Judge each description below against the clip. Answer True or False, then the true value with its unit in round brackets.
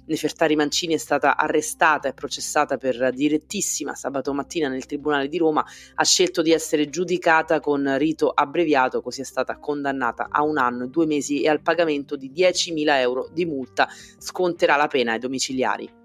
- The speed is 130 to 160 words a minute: False (170 wpm)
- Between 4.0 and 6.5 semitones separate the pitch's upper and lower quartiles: False (3.0 semitones)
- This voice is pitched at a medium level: True (150 Hz)